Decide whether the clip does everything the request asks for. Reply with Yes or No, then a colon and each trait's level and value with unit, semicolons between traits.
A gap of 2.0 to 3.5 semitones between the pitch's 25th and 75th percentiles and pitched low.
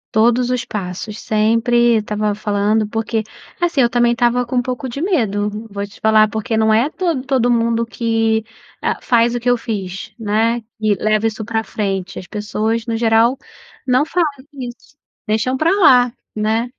No: narrow, 2.4 semitones; high, 230 Hz